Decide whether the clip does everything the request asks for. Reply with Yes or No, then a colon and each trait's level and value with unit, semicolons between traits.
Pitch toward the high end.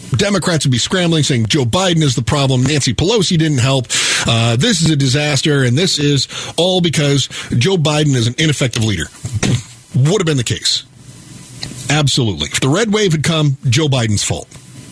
No: medium, 140 Hz